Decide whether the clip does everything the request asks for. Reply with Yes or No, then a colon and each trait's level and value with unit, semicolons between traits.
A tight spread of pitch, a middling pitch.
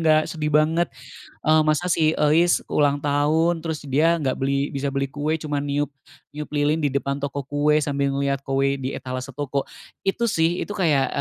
Yes: narrow, 2.2 semitones; medium, 145 Hz